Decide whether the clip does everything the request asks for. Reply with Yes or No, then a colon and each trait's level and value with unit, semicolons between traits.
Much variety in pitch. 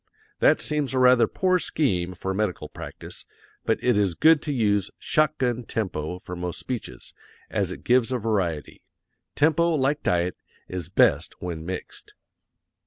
Yes: wide, 7.0 semitones